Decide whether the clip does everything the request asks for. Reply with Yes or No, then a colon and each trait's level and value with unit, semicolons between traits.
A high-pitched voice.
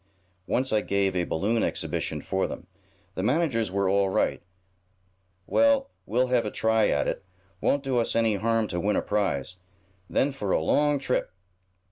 No: low, 110 Hz